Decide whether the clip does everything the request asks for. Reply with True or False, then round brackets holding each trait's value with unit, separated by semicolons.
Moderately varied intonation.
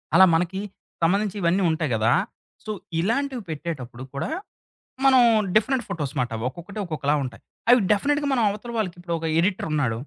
False (6.4 semitones)